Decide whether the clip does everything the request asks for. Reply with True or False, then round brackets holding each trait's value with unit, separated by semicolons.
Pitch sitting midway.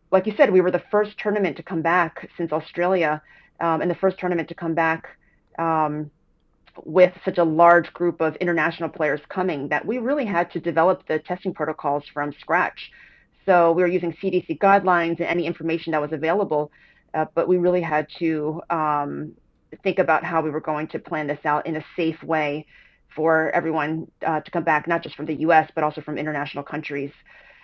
True (165 Hz)